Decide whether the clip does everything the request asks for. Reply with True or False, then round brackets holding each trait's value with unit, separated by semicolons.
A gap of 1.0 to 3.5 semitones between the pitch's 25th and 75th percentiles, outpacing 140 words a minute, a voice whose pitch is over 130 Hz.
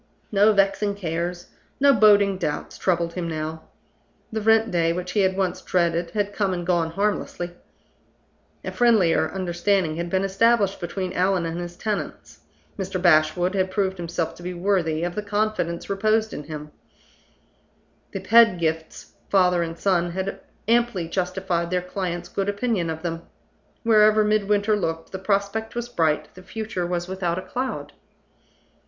True (3.1 semitones; 155 wpm; 185 Hz)